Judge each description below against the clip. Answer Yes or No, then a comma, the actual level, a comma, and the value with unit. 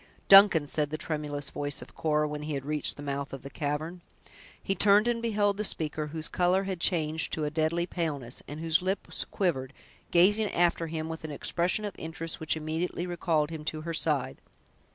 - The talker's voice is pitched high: No, medium, 160 Hz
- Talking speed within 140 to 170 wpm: No, average, 195 wpm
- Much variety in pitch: No, average, 3.0 semitones